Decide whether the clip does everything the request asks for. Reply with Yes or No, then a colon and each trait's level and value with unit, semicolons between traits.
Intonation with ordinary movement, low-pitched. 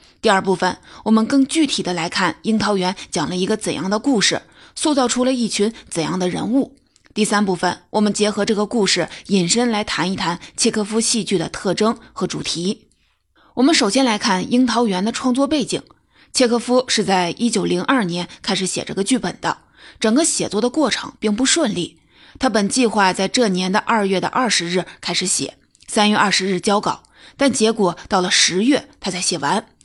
No: average, 4.7 semitones; high, 210 Hz